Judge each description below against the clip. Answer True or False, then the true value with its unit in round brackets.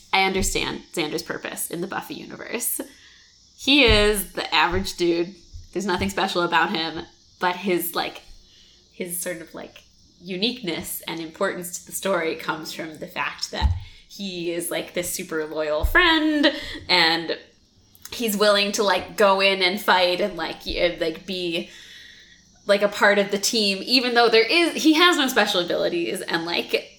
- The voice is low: False (185 Hz)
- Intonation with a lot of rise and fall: False (3.5 semitones)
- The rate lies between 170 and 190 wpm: False (160 wpm)